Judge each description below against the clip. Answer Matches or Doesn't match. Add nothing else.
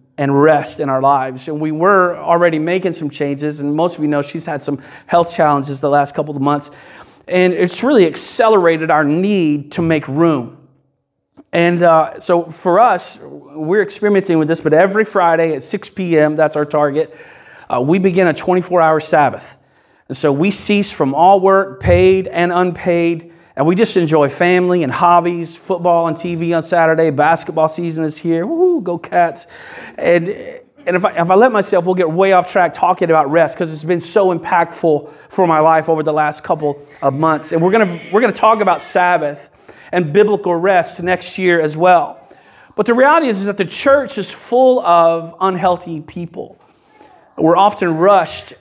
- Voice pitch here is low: Doesn't match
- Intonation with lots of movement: Doesn't match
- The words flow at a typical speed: Matches